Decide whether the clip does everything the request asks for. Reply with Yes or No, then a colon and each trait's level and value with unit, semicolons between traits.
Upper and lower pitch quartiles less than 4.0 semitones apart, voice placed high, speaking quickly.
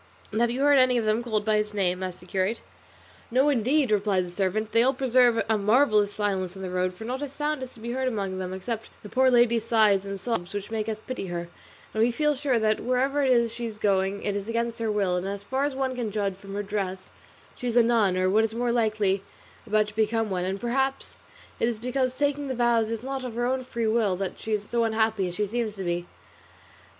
Yes: average, 3.6 semitones; high, 220 Hz; fast, 255 wpm